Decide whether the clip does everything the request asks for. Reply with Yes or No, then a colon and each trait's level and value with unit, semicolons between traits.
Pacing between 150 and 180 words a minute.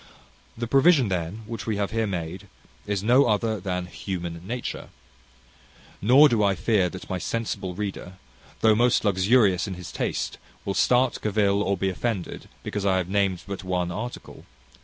Yes: average, 165 wpm